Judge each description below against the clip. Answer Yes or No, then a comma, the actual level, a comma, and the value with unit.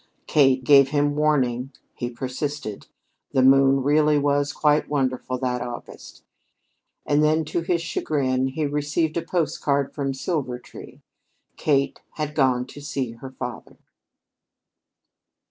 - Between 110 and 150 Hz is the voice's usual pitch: Yes, medium, 140 Hz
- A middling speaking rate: No, slow, 125 wpm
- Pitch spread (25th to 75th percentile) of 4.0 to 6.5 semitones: No, narrow, 2.5 semitones